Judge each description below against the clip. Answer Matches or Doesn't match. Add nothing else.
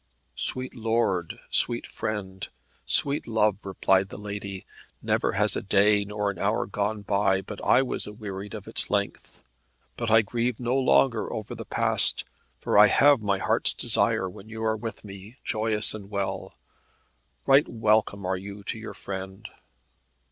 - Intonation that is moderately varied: Doesn't match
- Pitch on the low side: Matches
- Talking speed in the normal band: Matches